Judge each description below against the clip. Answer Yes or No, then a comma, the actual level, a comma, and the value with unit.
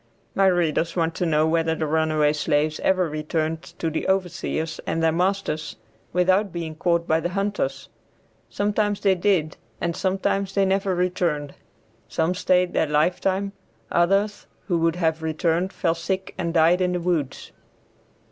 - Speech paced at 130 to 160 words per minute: Yes, average, 155 wpm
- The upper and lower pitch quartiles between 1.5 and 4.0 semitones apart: Yes, average, 2.9 semitones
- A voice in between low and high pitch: Yes, medium, 170 Hz